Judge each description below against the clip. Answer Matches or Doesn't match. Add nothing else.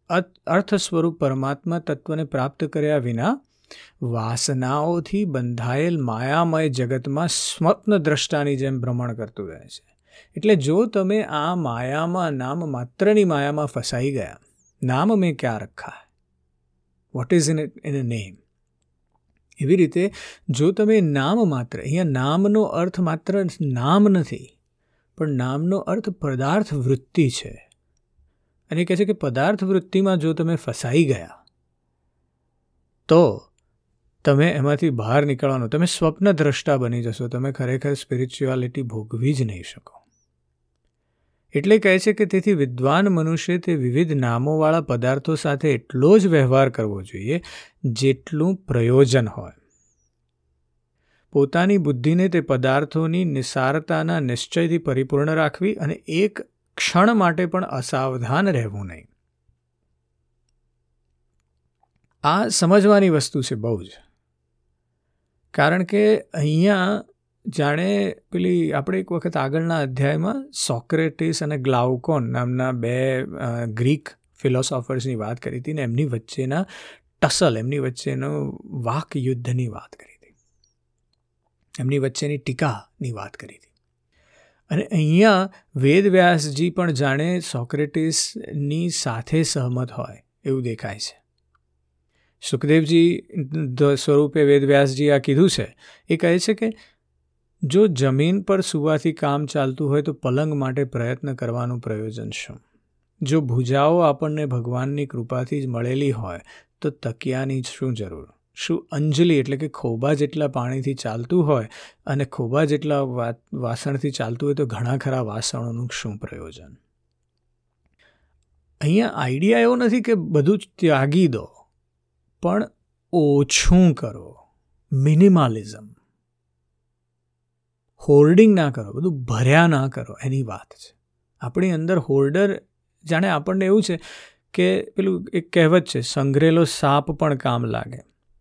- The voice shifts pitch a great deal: Matches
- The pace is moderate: Matches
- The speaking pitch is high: Doesn't match